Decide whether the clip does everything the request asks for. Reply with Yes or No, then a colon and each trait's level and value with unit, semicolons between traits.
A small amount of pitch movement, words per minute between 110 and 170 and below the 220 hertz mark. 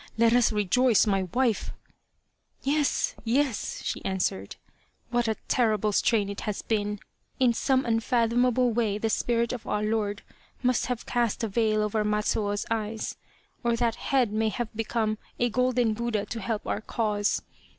No: narrow, 2.3 semitones; average, 165 wpm; high, 225 Hz